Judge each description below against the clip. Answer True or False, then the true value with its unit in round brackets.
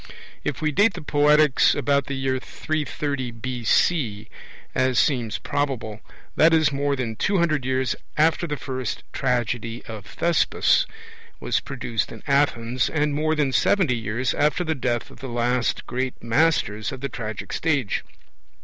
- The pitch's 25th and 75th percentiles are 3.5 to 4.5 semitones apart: True (3.9 semitones)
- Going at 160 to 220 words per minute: False (150 wpm)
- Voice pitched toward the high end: False (135 Hz)